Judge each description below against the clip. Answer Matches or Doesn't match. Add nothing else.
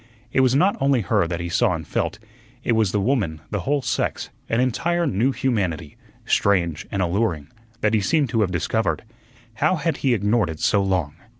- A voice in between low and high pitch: Doesn't match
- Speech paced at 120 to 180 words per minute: Doesn't match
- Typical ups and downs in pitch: Doesn't match